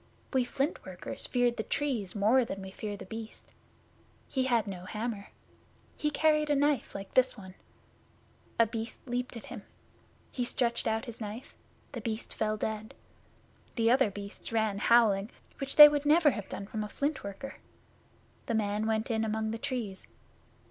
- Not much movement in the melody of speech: No, average, 3.6 semitones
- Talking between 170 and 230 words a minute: Yes, average, 175 wpm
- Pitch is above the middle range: Yes, high, 225 Hz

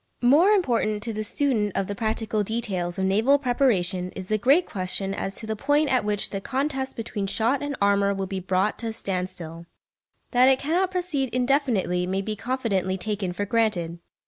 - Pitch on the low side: No, high, 215 Hz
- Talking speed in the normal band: Yes, average, 190 wpm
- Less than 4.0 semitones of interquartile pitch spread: No, average, 5.3 semitones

